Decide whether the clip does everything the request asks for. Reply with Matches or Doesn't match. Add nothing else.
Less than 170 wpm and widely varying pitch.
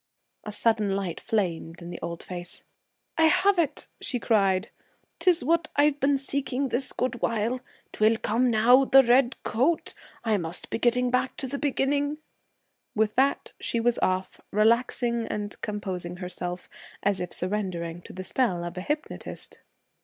Matches